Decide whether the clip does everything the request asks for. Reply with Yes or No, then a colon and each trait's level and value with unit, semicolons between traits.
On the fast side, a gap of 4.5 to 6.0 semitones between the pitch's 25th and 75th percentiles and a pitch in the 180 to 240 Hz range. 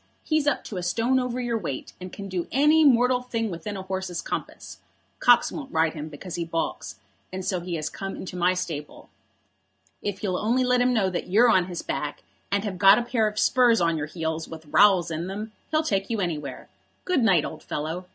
Yes: fast, 220 wpm; wide, 5.6 semitones; high, 190 Hz